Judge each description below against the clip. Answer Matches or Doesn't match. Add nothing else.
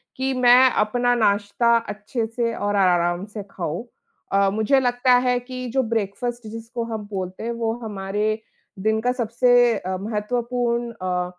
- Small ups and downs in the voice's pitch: Doesn't match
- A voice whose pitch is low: Doesn't match